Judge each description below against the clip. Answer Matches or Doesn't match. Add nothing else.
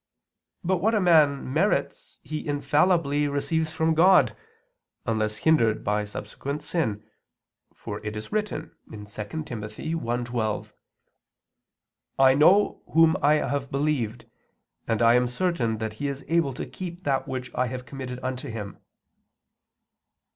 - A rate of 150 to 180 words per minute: Doesn't match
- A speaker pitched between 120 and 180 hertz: Matches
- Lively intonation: Matches